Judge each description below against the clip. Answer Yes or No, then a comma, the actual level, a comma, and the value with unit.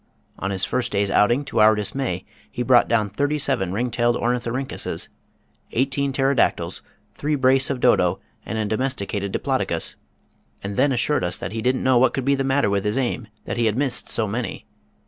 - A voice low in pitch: Yes, low, 120 Hz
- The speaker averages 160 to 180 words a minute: No, average, 190 wpm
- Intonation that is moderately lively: Yes, average, 4.2 semitones